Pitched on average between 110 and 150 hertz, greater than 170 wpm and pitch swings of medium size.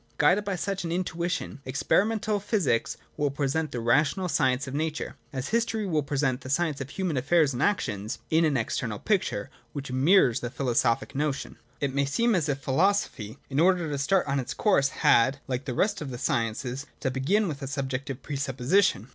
Yes: medium, 140 Hz; average, 200 wpm; average, 5.0 semitones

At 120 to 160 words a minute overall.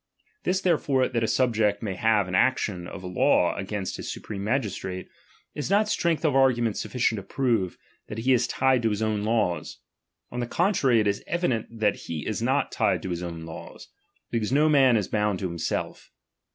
No: average, 195 wpm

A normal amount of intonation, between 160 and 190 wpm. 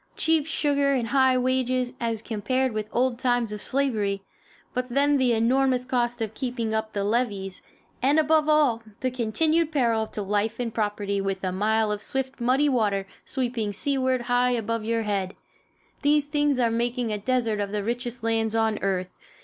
Yes: average, 3.3 semitones; average, 175 wpm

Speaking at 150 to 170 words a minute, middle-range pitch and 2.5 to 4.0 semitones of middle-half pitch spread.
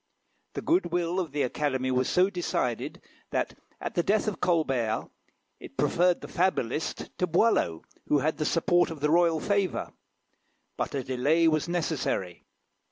No: average, 155 wpm; medium, 160 Hz; average, 4.9 semitones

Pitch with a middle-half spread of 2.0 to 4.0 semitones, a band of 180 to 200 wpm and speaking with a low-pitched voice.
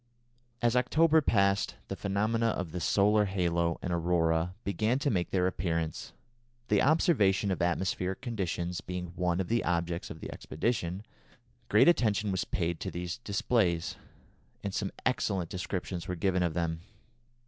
No: average, 3.5 semitones; average, 150 wpm; very low, 95 Hz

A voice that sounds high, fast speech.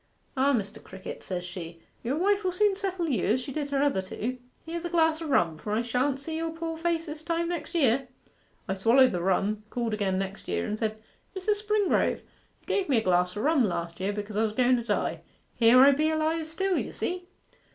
Yes: very high, 265 Hz; fast, 225 wpm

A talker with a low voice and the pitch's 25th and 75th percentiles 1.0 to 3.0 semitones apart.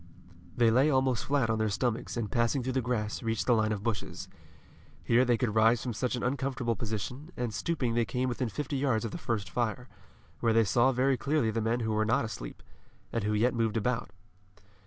Yes: low, 120 Hz; narrow, 2.5 semitones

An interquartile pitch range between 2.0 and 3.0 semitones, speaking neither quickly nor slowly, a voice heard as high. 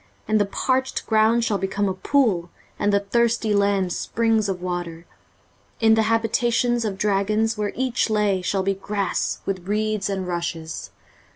Yes: average, 2.7 semitones; average, 165 wpm; high, 205 Hz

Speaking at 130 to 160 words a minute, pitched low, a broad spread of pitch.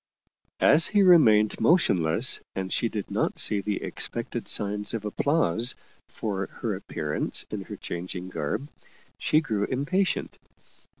Yes: slow, 135 wpm; low, 105 Hz; wide, 7.4 semitones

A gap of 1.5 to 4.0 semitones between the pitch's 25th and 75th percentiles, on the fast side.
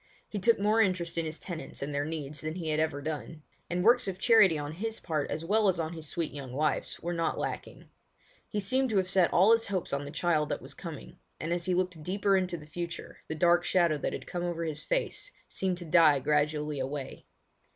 Yes: average, 3.5 semitones; fast, 235 wpm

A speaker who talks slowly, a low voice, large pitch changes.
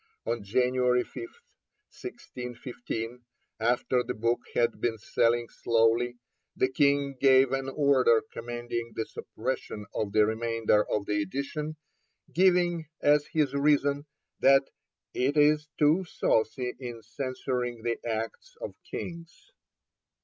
No: slow, 120 wpm; low, 125 Hz; average, 3.9 semitones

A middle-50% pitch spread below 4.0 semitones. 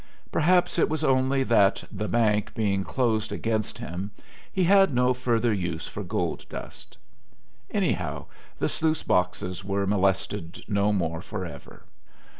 No: average, 4.7 semitones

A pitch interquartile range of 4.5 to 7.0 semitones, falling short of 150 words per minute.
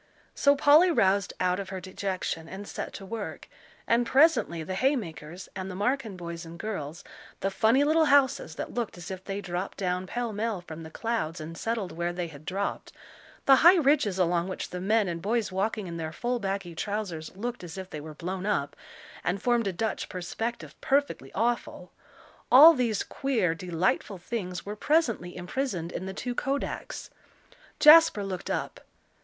No: average, 5.2 semitones; average, 180 wpm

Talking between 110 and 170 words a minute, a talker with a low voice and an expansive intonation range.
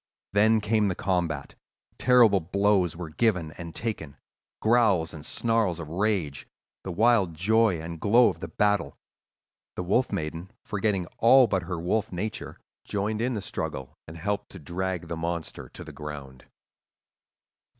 No: average, 150 wpm; very low, 95 Hz; average, 4.7 semitones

